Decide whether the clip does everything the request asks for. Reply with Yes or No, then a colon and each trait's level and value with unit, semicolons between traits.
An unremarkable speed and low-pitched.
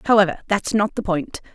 No: average, 195 wpm; high, 195 Hz